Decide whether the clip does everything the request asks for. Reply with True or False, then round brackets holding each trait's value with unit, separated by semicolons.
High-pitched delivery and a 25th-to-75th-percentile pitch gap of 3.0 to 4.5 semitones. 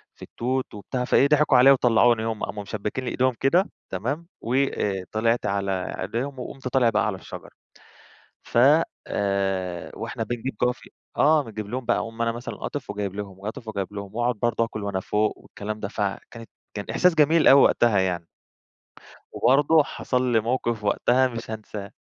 False (115 Hz; 3.9 semitones)